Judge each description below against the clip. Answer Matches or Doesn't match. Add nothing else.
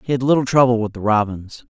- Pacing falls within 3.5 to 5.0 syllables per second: Doesn't match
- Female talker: Doesn't match